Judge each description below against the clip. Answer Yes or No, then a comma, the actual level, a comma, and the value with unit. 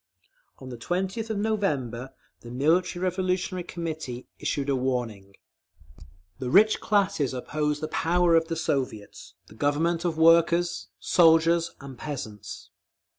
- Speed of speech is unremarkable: No, slow, 125 wpm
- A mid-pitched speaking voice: Yes, medium, 160 Hz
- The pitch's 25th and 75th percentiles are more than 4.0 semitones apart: Yes, average, 5.2 semitones